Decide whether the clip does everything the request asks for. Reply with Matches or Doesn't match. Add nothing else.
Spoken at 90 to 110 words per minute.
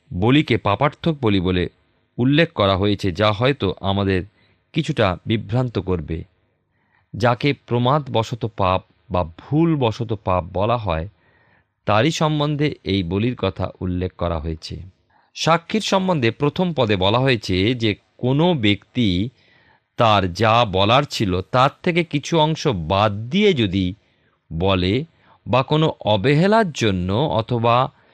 Doesn't match